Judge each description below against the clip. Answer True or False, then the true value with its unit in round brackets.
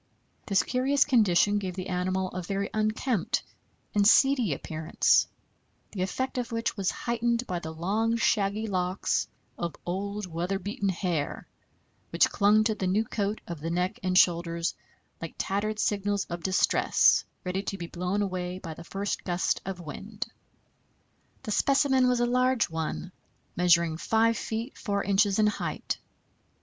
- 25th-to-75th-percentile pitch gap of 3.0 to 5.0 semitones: True (3.6 semitones)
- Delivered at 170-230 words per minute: False (155 wpm)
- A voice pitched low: False (195 Hz)